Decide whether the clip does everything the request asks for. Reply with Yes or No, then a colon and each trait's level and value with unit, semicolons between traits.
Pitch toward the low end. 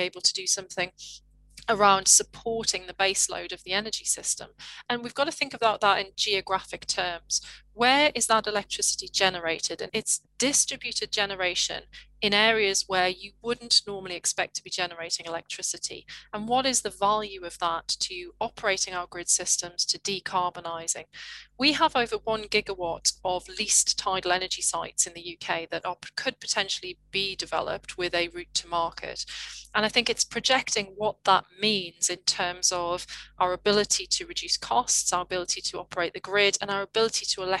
No: high, 195 Hz